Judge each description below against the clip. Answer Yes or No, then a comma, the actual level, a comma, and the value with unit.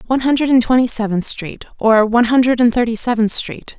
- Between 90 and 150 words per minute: No, average, 190 wpm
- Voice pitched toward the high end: Yes, high, 235 Hz